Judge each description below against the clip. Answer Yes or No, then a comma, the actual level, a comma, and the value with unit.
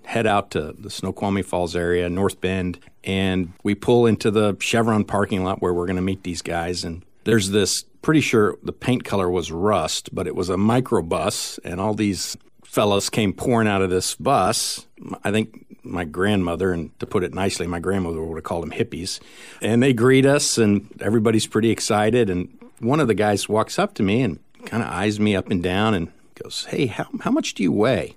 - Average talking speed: No, fast, 210 wpm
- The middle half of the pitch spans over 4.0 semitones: No, average, 3.4 semitones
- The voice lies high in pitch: No, low, 100 Hz